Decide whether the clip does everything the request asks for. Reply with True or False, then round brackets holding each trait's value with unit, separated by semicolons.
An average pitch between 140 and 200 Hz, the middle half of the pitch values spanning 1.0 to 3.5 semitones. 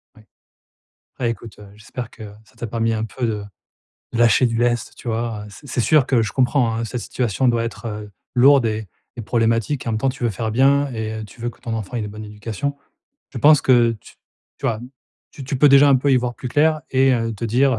False (120 Hz; 2.8 semitones)